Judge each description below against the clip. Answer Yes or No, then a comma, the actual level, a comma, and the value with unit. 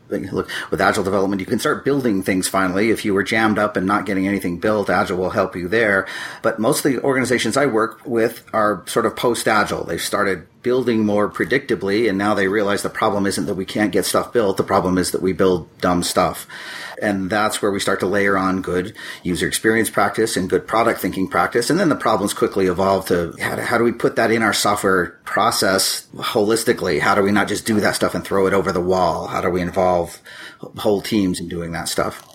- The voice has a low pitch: Yes, very low, 95 Hz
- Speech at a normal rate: No, fast, 225 wpm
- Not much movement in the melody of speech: Yes, narrow, 2.2 semitones